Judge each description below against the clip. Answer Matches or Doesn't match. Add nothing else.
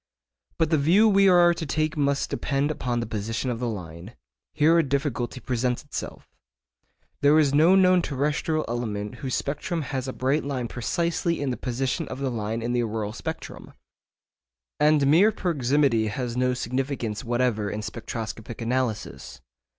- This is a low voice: Matches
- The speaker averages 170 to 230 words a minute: Doesn't match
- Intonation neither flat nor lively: Matches